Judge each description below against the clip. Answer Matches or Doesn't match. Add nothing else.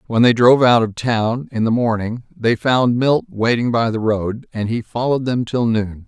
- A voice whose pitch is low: Matches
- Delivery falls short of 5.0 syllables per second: Matches